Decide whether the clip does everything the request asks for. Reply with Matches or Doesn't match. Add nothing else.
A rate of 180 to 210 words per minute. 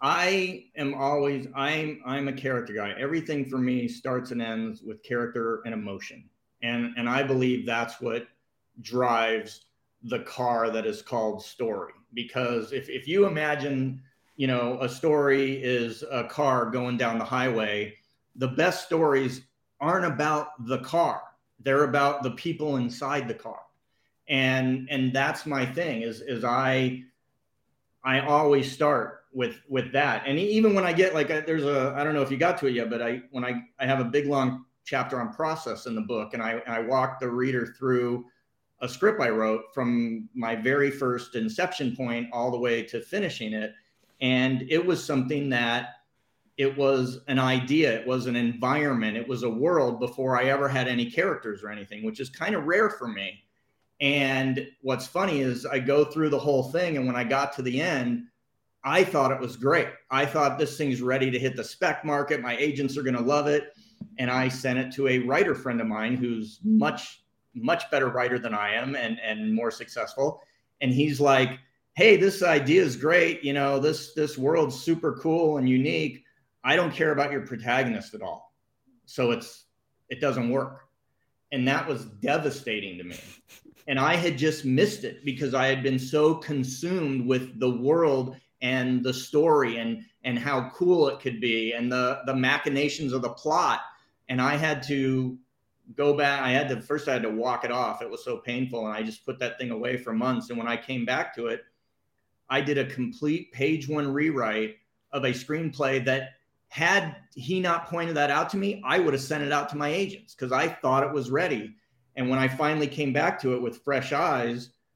Matches